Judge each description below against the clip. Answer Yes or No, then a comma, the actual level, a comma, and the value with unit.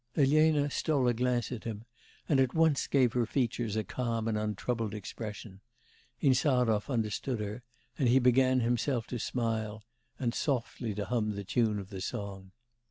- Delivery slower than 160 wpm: No, average, 165 wpm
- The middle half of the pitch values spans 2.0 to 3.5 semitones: Yes, average, 3.2 semitones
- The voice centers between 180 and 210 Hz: No, low, 120 Hz